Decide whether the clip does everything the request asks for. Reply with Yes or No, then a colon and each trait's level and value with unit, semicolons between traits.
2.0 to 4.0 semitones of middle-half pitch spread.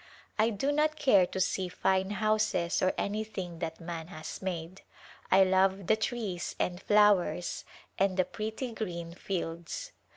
Yes: average, 3.4 semitones